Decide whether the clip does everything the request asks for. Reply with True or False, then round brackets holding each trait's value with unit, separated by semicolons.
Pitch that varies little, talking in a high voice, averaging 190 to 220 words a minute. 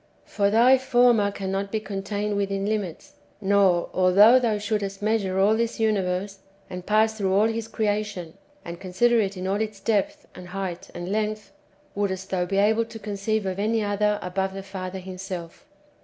False (2.2 semitones; 200 Hz; 175 wpm)